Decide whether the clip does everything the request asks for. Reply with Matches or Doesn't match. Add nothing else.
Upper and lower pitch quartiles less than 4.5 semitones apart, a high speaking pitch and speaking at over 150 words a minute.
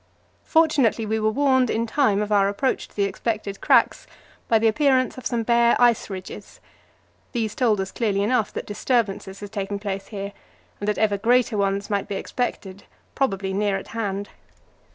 Matches